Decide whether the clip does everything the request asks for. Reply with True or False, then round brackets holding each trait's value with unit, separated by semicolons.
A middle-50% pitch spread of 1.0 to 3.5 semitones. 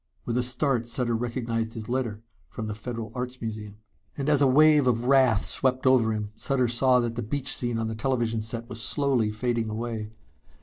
True (2.4 semitones)